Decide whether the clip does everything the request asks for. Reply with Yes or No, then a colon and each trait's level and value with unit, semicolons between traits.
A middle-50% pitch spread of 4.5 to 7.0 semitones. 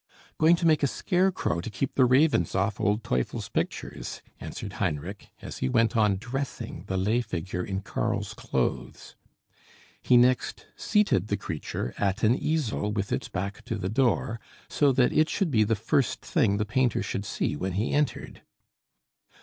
Yes: wide, 5.5 semitones